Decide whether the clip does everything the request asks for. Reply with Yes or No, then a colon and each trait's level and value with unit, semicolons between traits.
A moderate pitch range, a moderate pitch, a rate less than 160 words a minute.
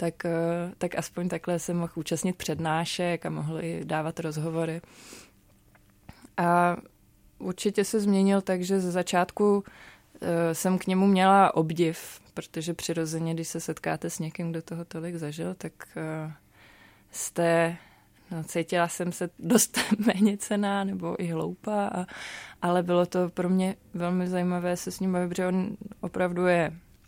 No: narrow, 2.2 semitones; medium, 175 Hz; average, 140 wpm